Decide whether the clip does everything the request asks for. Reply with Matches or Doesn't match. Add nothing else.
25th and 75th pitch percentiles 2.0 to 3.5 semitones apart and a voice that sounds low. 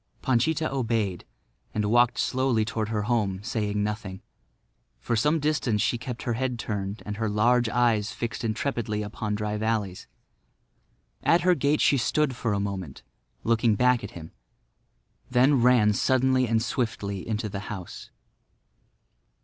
Matches